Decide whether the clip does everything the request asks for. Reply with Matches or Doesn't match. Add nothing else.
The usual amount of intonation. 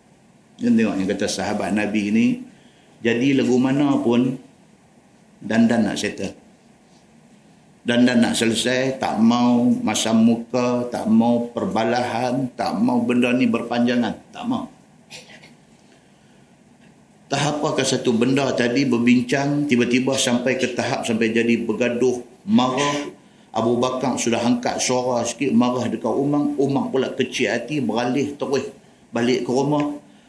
Matches